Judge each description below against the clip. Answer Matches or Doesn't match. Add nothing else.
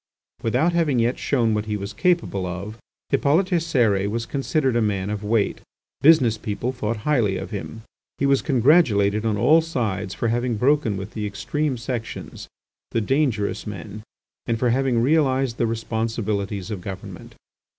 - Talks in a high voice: Doesn't match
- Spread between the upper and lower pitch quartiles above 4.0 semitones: Matches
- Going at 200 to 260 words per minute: Doesn't match